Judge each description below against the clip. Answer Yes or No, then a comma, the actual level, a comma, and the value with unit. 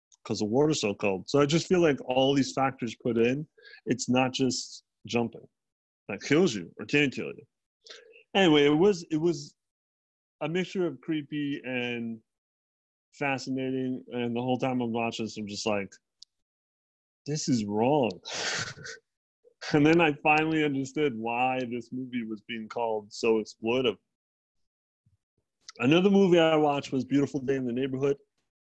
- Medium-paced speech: Yes, average, 150 wpm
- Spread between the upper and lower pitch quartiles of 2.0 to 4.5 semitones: No, average, 5.3 semitones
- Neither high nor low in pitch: No, low, 130 Hz